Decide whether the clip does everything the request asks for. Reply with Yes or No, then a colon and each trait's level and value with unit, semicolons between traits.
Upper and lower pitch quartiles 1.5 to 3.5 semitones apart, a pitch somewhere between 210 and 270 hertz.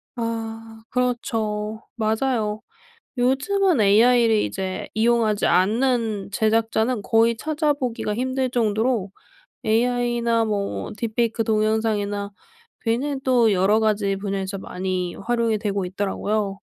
Yes: narrow, 2.6 semitones; high, 225 Hz